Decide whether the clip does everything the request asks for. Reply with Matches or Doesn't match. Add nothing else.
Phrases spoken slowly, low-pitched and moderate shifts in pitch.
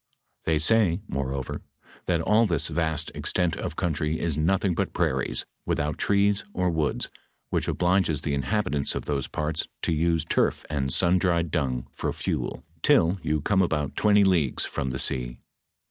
Doesn't match